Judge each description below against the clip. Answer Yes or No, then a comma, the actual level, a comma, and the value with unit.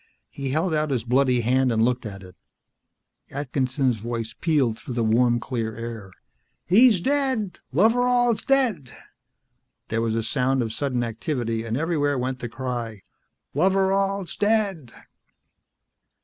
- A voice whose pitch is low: Yes, low, 130 Hz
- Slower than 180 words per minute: Yes, slow, 135 wpm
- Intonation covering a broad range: Yes, wide, 7.4 semitones